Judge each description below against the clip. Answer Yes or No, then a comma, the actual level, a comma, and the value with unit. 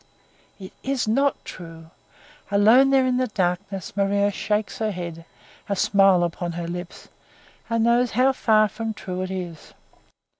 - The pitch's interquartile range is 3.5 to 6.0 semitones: Yes, average, 4.3 semitones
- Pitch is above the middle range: Yes, high, 200 Hz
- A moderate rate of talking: Yes, average, 150 wpm